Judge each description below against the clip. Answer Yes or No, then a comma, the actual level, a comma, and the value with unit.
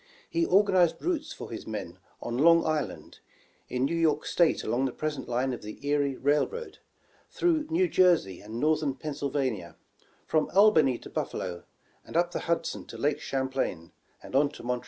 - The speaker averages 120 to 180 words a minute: Yes, average, 170 wpm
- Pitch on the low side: No, medium, 145 Hz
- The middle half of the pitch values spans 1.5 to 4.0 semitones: No, average, 5.2 semitones